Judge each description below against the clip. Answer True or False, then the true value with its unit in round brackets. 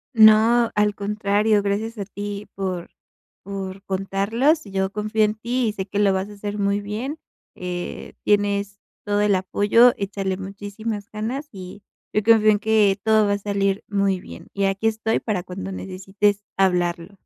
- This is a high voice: True (205 Hz)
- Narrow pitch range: True (1.6 semitones)